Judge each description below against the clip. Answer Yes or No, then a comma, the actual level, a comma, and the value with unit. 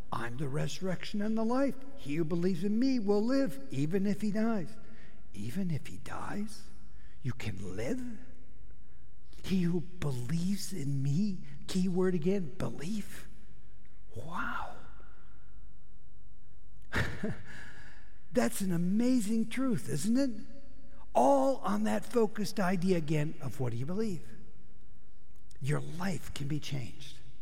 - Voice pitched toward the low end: No, high, 190 Hz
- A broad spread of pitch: Yes, wide, 6.9 semitones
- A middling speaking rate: No, slow, 125 wpm